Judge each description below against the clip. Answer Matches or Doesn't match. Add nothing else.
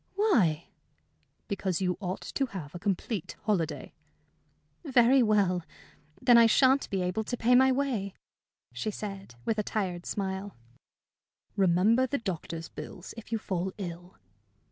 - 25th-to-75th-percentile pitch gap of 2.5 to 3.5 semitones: Doesn't match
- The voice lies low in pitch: Doesn't match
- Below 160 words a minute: Matches